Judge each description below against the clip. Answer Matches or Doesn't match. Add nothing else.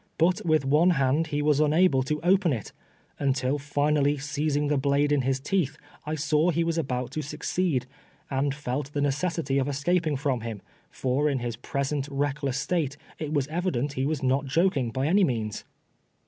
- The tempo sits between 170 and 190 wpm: Matches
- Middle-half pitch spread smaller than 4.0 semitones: Matches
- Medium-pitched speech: Matches